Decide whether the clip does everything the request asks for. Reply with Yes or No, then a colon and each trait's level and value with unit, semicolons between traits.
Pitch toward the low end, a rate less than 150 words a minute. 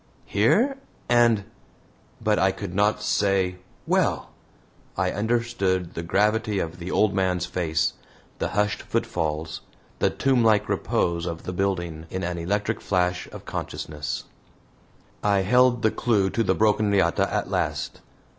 Yes: low, 100 Hz; slow, 135 wpm